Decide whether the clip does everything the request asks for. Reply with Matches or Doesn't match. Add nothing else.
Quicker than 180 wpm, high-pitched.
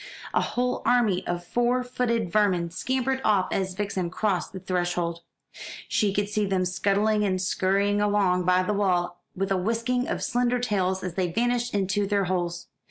Doesn't match